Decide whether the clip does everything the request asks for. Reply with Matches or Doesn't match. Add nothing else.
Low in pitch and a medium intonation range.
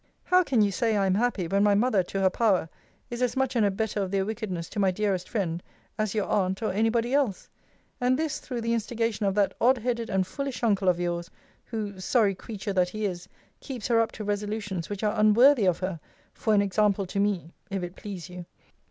Doesn't match